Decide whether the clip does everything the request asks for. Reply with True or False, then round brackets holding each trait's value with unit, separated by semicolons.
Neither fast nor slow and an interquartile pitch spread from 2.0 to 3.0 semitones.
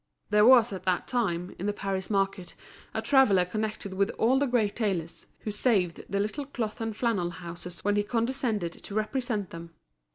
False (185 wpm; 3.9 semitones)